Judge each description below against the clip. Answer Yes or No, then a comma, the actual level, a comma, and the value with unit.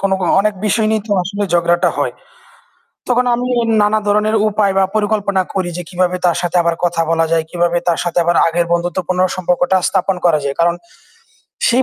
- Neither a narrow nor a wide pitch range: Yes, average, 3.2 semitones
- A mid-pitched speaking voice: Yes, medium, 180 Hz